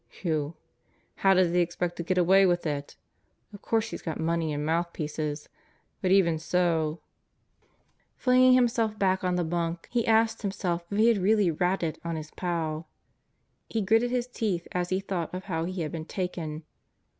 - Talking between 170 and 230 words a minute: Yes, average, 180 wpm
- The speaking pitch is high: No, medium, 180 Hz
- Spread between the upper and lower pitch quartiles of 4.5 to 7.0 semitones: No, average, 3.3 semitones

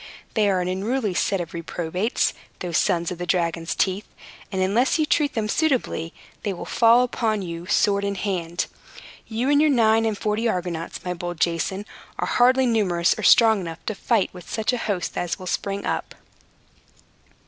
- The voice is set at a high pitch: Yes, high, 195 Hz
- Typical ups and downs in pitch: Yes, average, 4.3 semitones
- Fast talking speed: No, average, 180 wpm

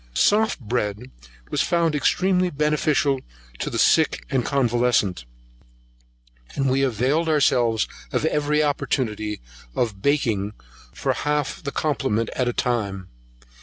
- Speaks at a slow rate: Yes, slow, 120 wpm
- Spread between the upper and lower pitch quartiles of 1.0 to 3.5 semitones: No, average, 4.9 semitones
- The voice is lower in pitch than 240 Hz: Yes, low, 135 Hz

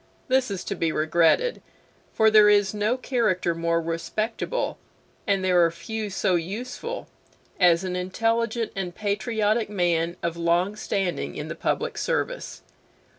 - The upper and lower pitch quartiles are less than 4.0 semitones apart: No, average, 4.4 semitones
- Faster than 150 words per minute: No, average, 140 wpm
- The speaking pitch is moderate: No, high, 195 Hz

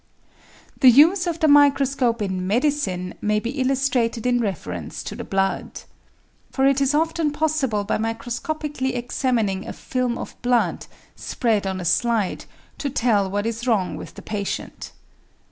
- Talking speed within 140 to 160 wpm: Yes, average, 150 wpm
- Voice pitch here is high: Yes, high, 240 Hz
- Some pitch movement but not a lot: Yes, average, 4.9 semitones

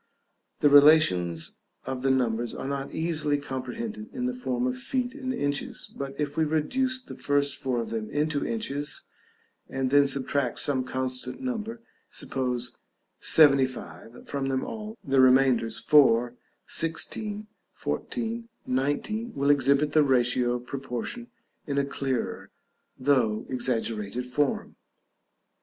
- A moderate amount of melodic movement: Yes, average, 3.9 semitones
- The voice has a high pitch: No, medium, 140 Hz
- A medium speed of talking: No, slow, 130 wpm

